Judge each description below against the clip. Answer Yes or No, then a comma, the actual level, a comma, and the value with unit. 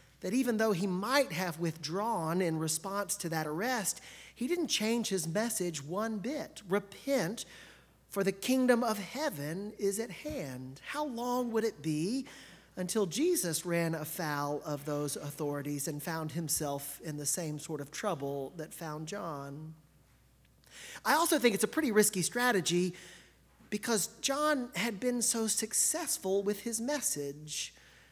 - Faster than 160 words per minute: No, average, 145 wpm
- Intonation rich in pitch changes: Yes, wide, 6.9 semitones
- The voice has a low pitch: No, high, 195 Hz